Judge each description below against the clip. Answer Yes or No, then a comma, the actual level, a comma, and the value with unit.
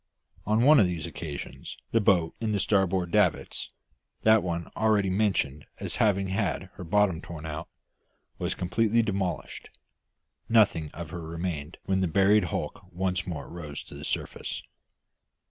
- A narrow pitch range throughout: No, average, 3.7 semitones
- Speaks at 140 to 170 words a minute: Yes, average, 150 wpm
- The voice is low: Yes, very low, 95 Hz